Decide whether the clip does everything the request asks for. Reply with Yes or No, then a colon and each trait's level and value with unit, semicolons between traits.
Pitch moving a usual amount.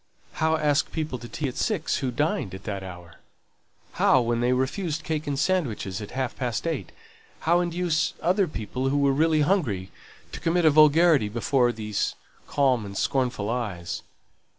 No: wide, 5.8 semitones